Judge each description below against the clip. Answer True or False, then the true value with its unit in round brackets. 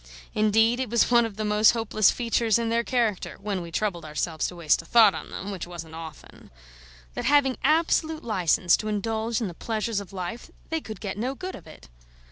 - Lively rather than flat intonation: False (4.2 semitones)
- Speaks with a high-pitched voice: True (215 Hz)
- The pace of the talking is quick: True (210 wpm)